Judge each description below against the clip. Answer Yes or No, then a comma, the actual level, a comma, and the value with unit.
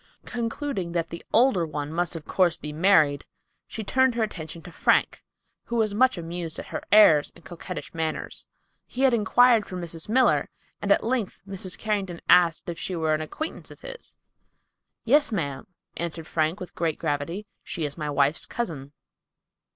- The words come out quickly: No, average, 175 wpm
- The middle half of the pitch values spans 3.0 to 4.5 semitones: No, wide, 5.5 semitones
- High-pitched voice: No, medium, 175 Hz